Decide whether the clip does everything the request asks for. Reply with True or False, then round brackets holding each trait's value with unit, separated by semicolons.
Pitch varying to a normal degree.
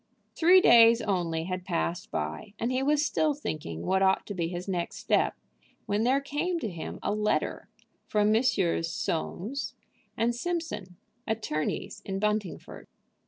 False (6.1 semitones)